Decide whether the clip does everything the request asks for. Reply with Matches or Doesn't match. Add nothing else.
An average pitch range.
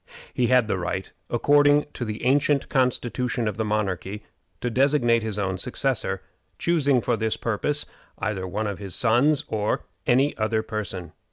Matches